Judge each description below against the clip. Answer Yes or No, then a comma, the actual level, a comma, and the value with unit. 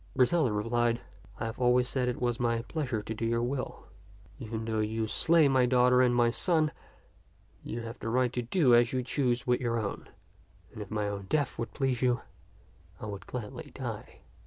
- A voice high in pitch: No, low, 120 Hz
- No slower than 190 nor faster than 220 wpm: Yes, average, 200 wpm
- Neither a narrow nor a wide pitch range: No, narrow, 2.0 semitones